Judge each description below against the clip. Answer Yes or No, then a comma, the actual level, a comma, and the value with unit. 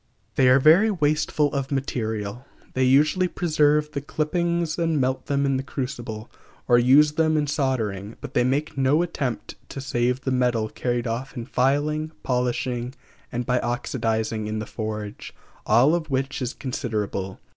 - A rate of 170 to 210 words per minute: No, average, 160 wpm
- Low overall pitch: Yes, low, 130 Hz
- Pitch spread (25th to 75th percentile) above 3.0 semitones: Yes, average, 3.8 semitones